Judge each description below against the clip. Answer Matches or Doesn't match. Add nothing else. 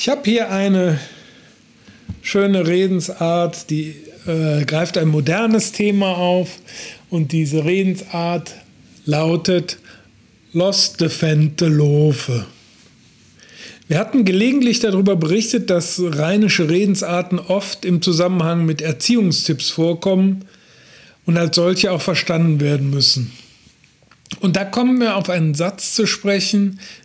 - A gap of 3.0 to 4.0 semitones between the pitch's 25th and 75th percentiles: Matches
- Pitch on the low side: Doesn't match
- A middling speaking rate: Doesn't match